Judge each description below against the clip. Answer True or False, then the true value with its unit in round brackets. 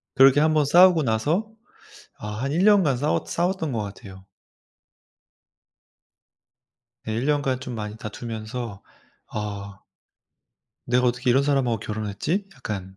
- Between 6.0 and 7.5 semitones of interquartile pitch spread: False (5.6 semitones)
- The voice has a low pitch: True (125 Hz)